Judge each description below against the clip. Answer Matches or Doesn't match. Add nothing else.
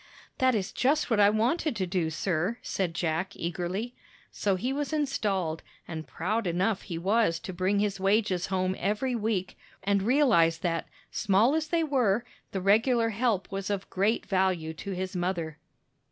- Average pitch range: Matches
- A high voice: Matches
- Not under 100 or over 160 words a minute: Doesn't match